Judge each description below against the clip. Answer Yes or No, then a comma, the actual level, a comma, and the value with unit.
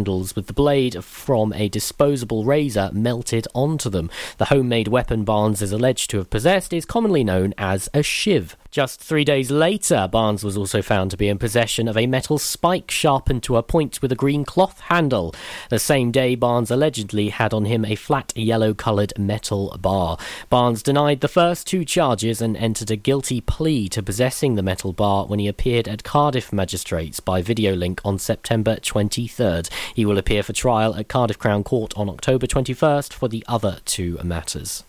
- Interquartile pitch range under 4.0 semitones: No, average, 4.7 semitones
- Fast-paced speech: No, average, 185 wpm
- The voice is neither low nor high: No, low, 115 Hz